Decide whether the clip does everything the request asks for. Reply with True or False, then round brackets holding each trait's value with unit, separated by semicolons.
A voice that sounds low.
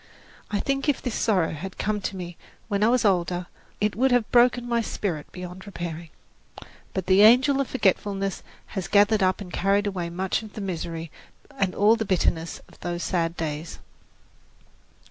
False (195 Hz)